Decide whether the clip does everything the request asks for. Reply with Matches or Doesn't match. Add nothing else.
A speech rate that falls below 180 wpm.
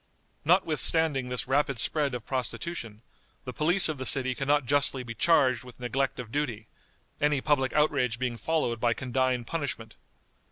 Matches